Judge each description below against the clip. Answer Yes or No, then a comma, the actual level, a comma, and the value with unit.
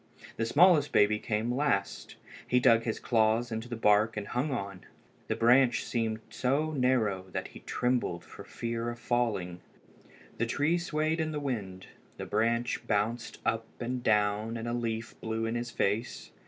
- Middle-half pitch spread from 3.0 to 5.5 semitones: No, narrow, 2.5 semitones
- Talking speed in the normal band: Yes, average, 170 wpm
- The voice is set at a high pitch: No, low, 115 Hz